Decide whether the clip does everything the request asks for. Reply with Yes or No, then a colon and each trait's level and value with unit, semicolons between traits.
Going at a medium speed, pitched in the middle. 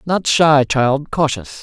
Yes: average, 150 wpm; medium, 145 Hz